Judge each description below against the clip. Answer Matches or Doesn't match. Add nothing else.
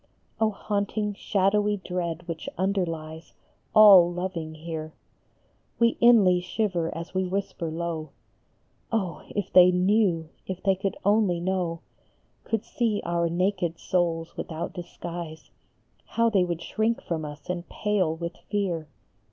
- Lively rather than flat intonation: Doesn't match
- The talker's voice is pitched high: Doesn't match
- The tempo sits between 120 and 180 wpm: Matches